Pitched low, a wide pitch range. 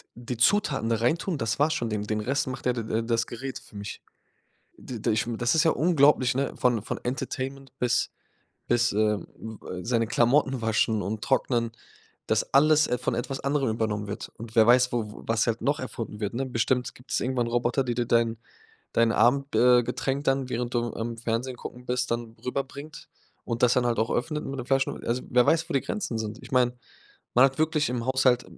No: low, 120 Hz; average, 2.7 semitones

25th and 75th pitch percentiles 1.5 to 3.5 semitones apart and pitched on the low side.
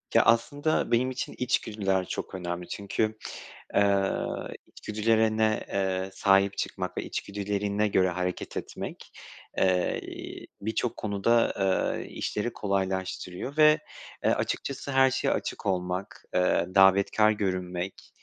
Yes: average, 2.8 semitones; low, 100 Hz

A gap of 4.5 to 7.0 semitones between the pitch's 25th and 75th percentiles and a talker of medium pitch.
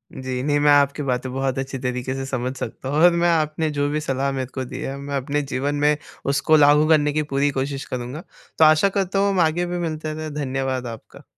No: narrow, 2.6 semitones; medium, 145 Hz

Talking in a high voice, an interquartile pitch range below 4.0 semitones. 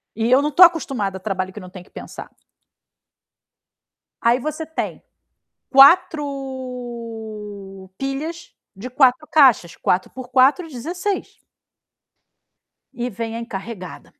No: very high, 250 Hz; average, 5.1 semitones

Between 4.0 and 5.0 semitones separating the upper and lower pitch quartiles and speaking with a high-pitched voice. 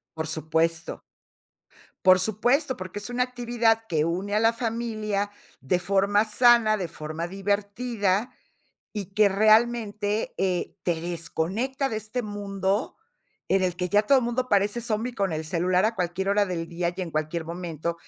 Yes: average, 4.3 semitones; high, 200 Hz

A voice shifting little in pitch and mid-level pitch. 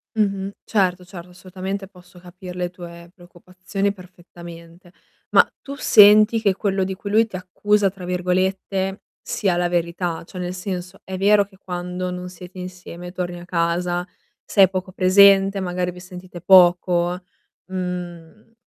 Yes: narrow, 1.6 semitones; medium, 180 Hz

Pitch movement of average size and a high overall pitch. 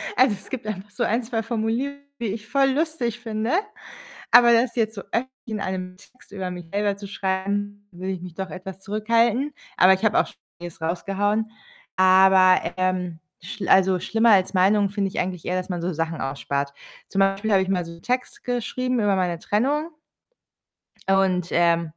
Yes: average, 3.5 semitones; high, 200 Hz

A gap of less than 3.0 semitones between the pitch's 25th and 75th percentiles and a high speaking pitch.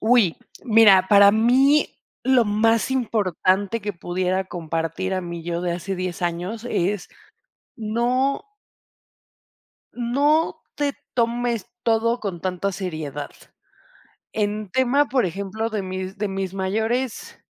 No: average, 4.1 semitones; high, 205 Hz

